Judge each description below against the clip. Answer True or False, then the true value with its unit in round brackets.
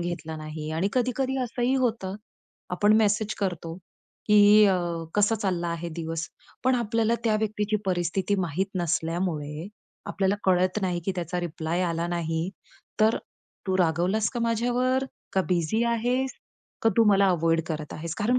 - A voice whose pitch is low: False (190 Hz)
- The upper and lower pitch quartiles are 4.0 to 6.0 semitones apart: True (4.6 semitones)